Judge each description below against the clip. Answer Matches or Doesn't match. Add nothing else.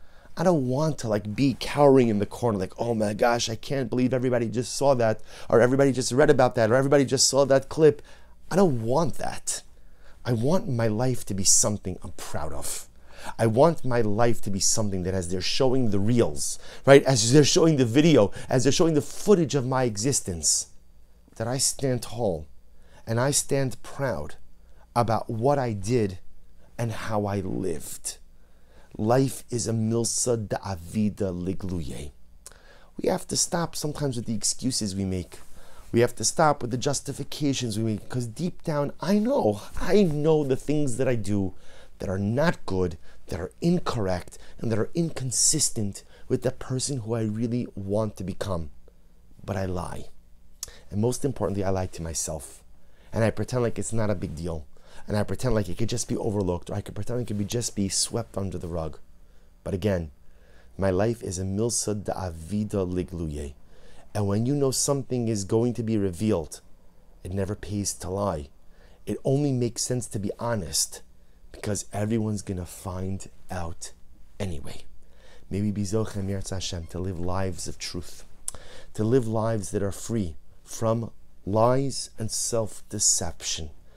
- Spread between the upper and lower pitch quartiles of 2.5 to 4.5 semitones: Doesn't match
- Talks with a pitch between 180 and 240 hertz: Doesn't match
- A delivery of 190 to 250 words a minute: Doesn't match